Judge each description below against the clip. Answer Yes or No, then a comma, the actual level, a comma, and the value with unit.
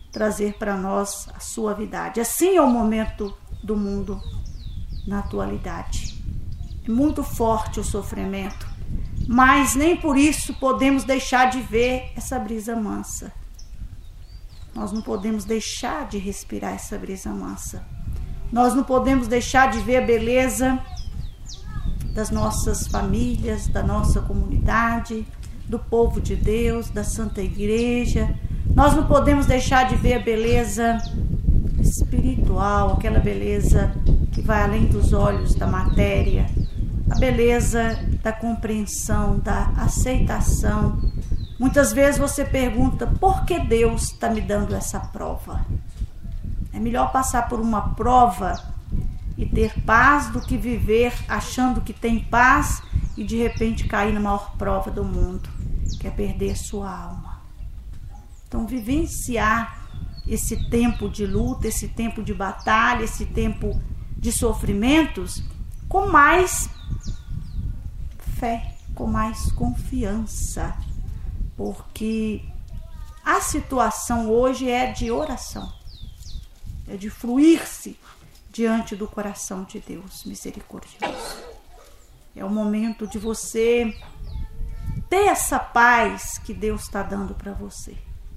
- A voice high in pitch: Yes, high, 205 Hz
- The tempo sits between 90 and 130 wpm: Yes, slow, 120 wpm